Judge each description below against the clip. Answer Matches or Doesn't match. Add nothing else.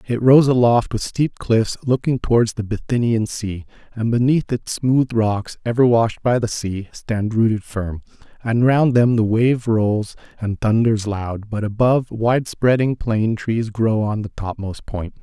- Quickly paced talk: Doesn't match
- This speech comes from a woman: Doesn't match